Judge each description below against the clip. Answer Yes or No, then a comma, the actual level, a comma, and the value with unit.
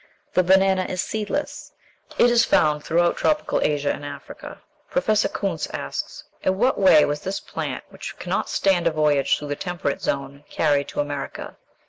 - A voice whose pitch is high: No, medium, 165 Hz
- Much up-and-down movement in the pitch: No, average, 4.8 semitones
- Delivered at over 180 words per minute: No, average, 165 wpm